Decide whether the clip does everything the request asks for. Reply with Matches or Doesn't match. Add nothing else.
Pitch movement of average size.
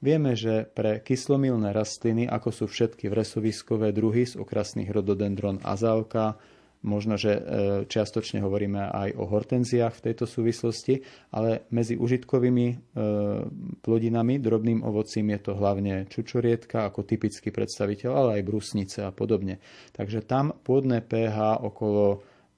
Doesn't match